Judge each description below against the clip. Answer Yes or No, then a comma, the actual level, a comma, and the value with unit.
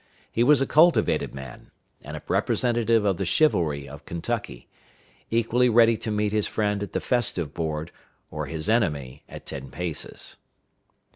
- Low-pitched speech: Yes, low, 100 Hz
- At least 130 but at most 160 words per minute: Yes, average, 155 wpm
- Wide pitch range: Yes, wide, 7.0 semitones